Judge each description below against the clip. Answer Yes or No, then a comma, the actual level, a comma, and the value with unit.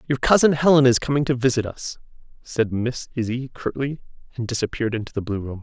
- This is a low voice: Yes, low, 125 Hz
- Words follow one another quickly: No, average, 190 wpm